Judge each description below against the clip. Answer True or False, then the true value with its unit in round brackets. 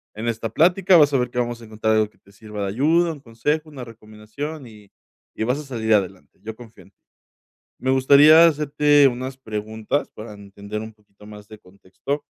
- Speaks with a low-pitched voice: True (115 Hz)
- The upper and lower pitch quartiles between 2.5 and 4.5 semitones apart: False (5.0 semitones)